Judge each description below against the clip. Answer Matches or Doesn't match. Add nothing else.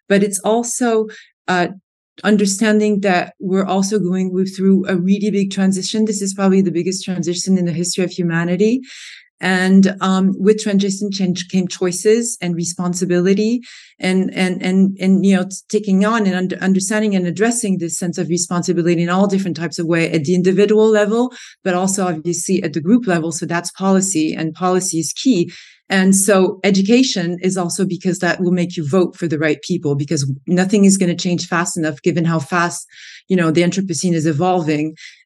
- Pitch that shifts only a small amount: Matches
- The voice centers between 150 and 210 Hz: Matches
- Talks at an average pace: Matches